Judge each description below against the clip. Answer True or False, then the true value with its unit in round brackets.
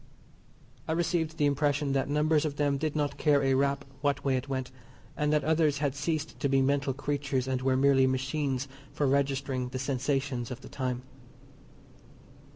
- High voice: False (140 Hz)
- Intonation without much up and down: True (1.9 semitones)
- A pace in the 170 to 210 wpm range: True (175 wpm)